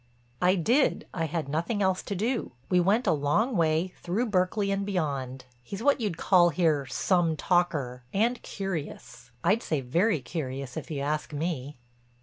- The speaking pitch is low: No, medium, 175 Hz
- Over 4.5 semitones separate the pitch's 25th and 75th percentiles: Yes, average, 5.3 semitones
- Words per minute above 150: Yes, average, 160 wpm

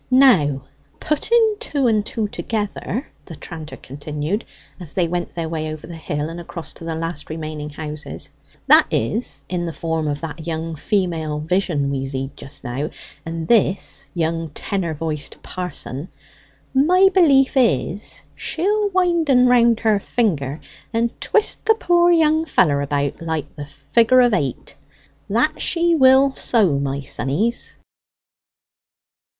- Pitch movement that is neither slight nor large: No, wide, 8.6 semitones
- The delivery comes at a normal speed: Yes, average, 145 wpm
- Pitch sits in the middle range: Yes, medium, 170 Hz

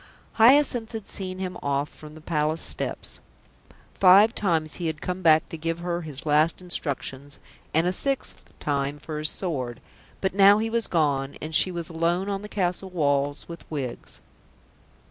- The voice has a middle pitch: Yes, medium, 165 Hz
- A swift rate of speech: No, average, 170 wpm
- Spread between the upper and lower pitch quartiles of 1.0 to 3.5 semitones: No, average, 3.9 semitones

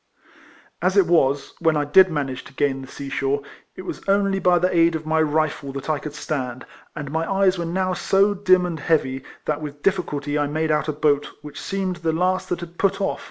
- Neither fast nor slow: No, fast, 225 wpm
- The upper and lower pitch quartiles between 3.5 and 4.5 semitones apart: Yes, average, 4.0 semitones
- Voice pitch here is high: No, medium, 160 Hz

